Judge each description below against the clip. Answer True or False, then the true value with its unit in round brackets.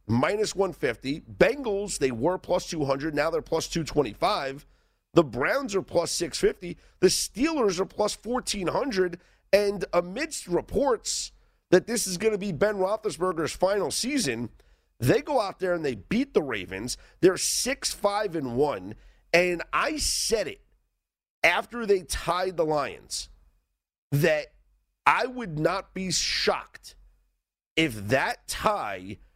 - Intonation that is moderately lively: False (6.0 semitones)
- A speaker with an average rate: False (130 wpm)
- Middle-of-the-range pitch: True (180 Hz)